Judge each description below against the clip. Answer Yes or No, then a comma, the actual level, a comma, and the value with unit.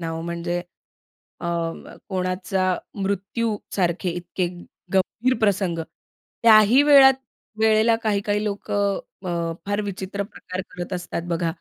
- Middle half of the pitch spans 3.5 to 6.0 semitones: No, average, 3.1 semitones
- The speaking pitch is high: Yes, high, 195 Hz